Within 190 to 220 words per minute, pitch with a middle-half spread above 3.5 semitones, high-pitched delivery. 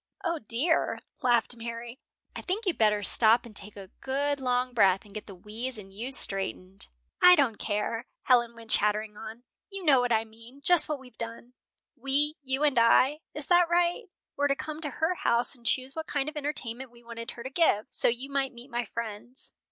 Yes: fast, 205 wpm; average, 4.1 semitones; high, 245 Hz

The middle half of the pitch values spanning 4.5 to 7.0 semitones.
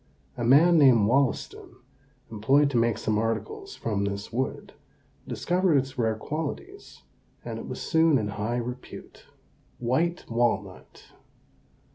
Yes: average, 4.8 semitones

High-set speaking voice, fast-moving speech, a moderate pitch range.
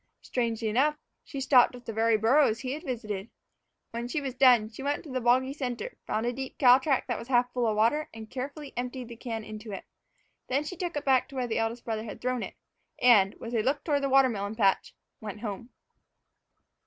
Yes: high, 245 Hz; fast, 220 wpm; average, 3.1 semitones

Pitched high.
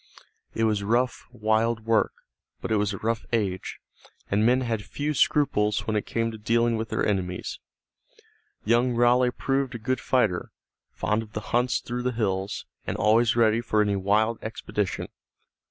No: low, 110 Hz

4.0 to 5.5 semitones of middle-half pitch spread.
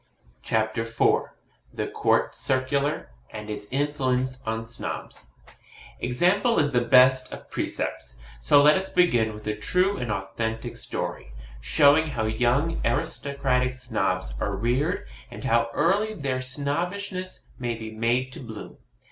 Yes: average, 4.7 semitones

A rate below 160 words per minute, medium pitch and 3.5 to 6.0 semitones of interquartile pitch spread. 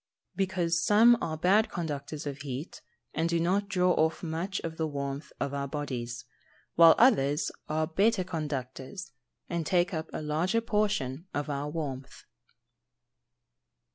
Yes: average, 145 wpm; medium, 160 Hz; average, 4.3 semitones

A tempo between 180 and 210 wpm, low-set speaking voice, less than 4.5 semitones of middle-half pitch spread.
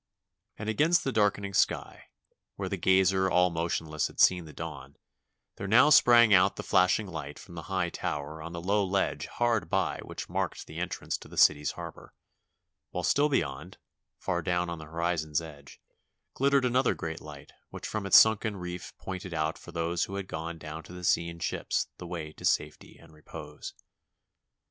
Yes: average, 185 wpm; very low, 90 Hz; average, 3.6 semitones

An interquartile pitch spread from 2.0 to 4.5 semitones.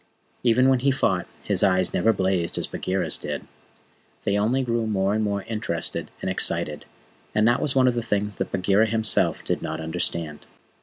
Yes: average, 3.9 semitones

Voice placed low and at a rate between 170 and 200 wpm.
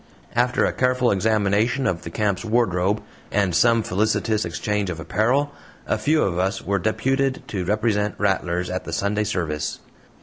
No: low, 105 Hz; average, 160 wpm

